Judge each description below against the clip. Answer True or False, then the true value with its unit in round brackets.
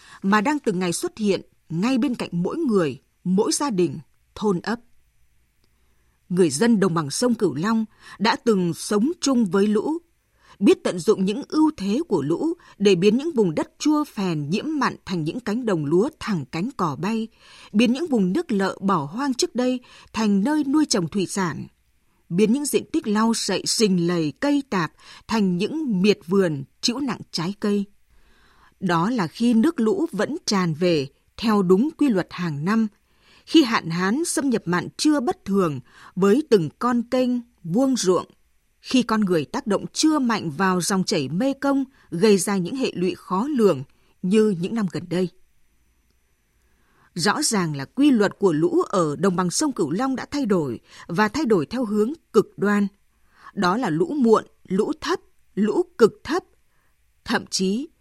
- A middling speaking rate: True (180 wpm)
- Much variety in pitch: True (6.0 semitones)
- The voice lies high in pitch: True (205 Hz)